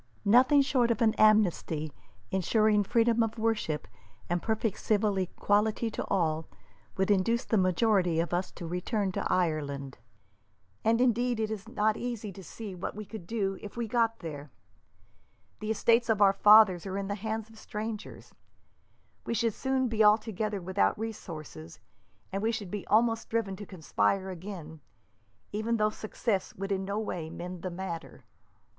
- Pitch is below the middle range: No, high, 210 Hz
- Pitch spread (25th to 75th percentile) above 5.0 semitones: No, average, 3.4 semitones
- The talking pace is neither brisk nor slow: Yes, average, 165 wpm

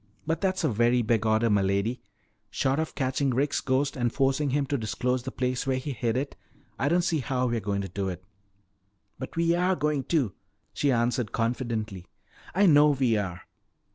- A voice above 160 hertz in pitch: No, low, 130 Hz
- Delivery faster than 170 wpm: Yes, average, 190 wpm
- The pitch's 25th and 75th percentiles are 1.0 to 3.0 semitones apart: No, average, 4.2 semitones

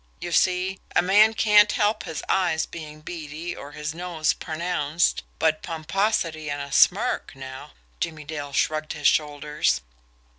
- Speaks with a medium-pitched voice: Yes, medium, 155 Hz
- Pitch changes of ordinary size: Yes, average, 3.3 semitones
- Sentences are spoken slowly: No, average, 150 wpm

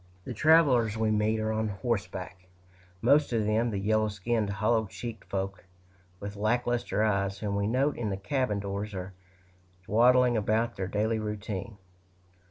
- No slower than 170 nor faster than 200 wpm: No, average, 160 wpm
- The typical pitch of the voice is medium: No, low, 110 Hz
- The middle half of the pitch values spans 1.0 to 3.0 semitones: Yes, average, 2.7 semitones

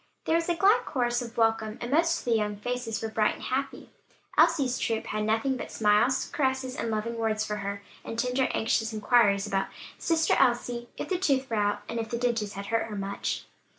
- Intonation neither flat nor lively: Yes, average, 3.4 semitones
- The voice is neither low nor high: No, high, 230 Hz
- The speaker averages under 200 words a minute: No, fast, 205 wpm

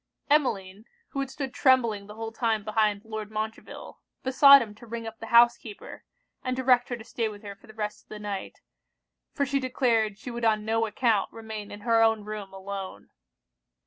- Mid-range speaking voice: No, high, 225 Hz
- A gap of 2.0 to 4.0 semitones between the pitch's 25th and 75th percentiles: Yes, narrow, 2.4 semitones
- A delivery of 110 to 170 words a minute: No, average, 195 wpm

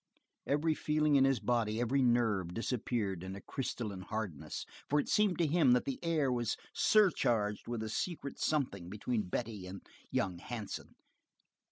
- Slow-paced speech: No, average, 160 wpm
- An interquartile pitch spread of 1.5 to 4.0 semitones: No, average, 5.2 semitones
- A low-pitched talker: Yes, low, 120 Hz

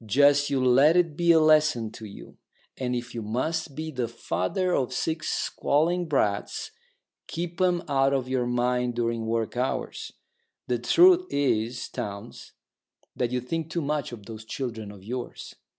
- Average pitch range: Yes, average, 4.9 semitones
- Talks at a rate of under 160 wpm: No, average, 165 wpm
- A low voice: Yes, low, 130 Hz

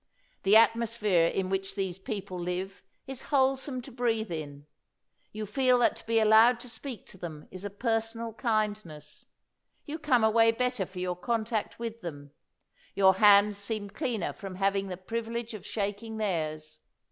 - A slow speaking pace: No, average, 180 wpm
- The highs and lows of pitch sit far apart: No, average, 3.6 semitones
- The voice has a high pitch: Yes, high, 215 Hz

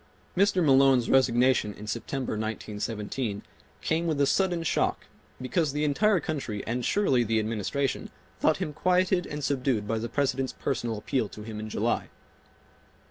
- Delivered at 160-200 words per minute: No, average, 150 wpm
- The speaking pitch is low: Yes, low, 130 Hz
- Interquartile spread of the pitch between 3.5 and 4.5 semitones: No, average, 5.1 semitones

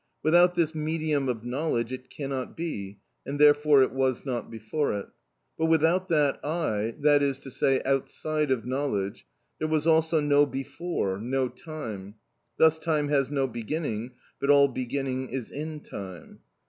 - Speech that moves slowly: No, average, 160 wpm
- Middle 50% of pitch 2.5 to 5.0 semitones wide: Yes, average, 3.7 semitones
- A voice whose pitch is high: No, medium, 140 Hz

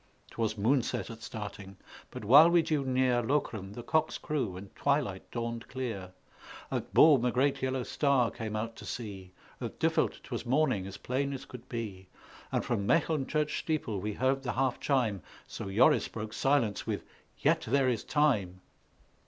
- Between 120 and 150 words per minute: No, average, 170 wpm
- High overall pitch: No, low, 120 Hz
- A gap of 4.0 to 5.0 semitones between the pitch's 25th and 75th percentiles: Yes, average, 4.7 semitones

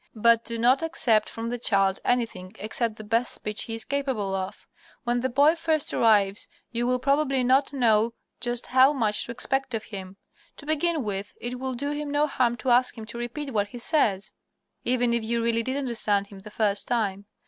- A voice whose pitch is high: Yes, high, 235 Hz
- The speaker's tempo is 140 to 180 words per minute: No, fast, 205 wpm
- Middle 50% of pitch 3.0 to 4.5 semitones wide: Yes, average, 3.6 semitones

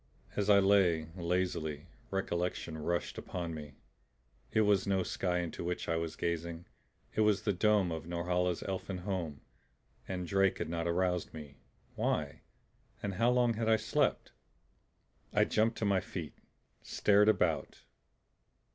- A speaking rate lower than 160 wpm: Yes, average, 145 wpm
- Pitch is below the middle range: Yes, very low, 90 Hz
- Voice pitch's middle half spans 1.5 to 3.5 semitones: Yes, average, 2.9 semitones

